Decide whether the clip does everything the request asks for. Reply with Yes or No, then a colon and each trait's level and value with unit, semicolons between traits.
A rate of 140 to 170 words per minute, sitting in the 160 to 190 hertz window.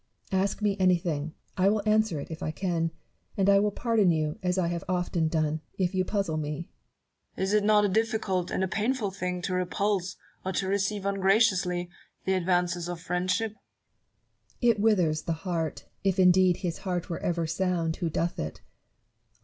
No: average, 190 wpm; medium, 185 Hz